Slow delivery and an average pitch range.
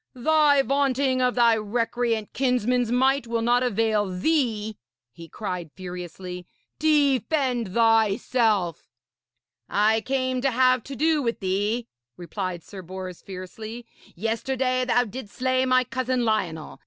Yes: slow, 125 wpm; average, 4.1 semitones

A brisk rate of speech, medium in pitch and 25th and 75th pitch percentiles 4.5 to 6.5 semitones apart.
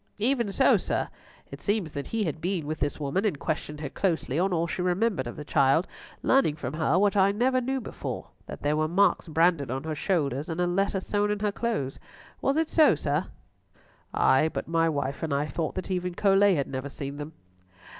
Yes: fast, 215 wpm; medium, 170 Hz; average, 5.2 semitones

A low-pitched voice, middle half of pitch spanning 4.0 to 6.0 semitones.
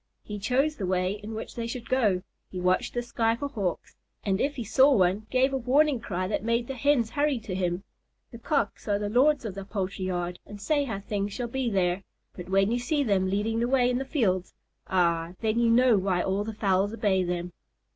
No: high, 215 Hz; average, 4.6 semitones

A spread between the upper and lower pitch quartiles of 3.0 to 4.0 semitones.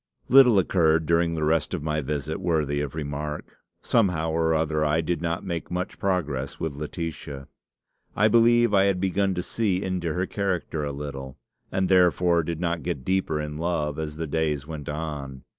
Yes: average, 3.4 semitones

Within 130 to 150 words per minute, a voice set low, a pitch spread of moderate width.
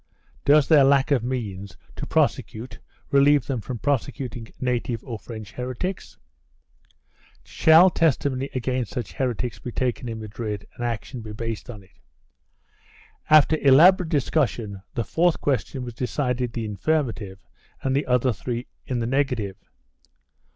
Yes: average, 140 wpm; low, 125 Hz; average, 3.7 semitones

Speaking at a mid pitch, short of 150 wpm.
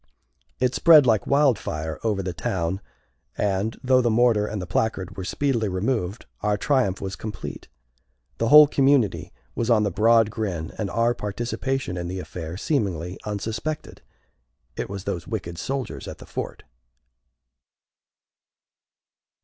No: low, 105 Hz; average, 140 wpm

